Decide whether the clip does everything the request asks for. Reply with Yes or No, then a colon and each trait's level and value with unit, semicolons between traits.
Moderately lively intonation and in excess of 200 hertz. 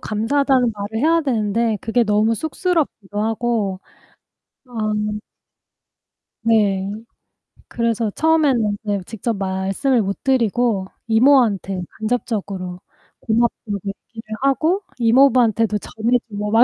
Yes: average, 3.3 semitones; high, 225 Hz